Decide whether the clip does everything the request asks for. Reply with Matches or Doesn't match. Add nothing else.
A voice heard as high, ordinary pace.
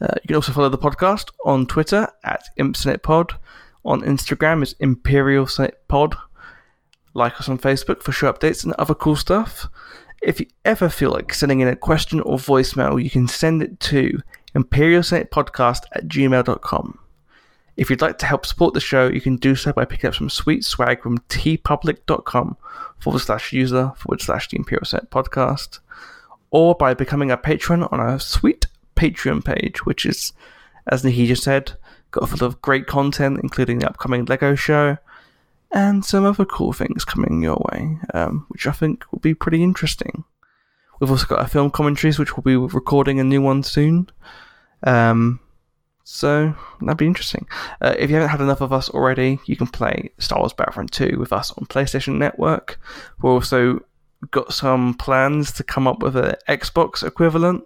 Doesn't match